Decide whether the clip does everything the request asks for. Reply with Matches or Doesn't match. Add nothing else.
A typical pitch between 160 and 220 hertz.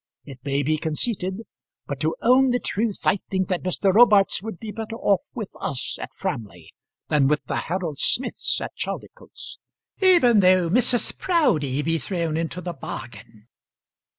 Matches